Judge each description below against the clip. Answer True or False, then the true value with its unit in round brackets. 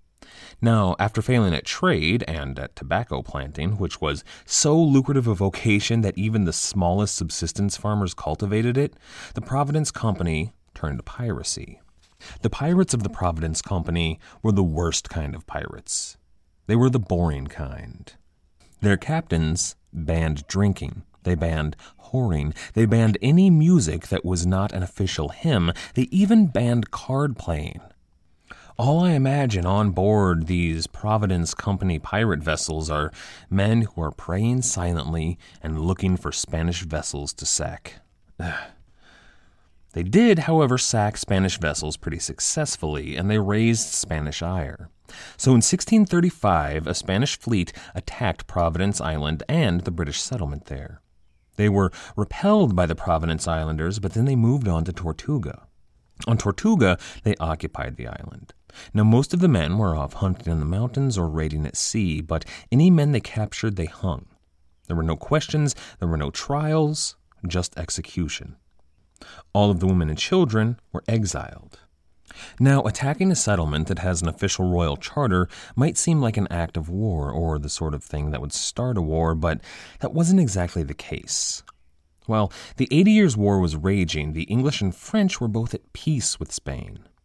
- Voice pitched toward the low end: True (95 Hz)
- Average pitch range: False (6.0 semitones)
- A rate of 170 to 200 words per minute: False (155 wpm)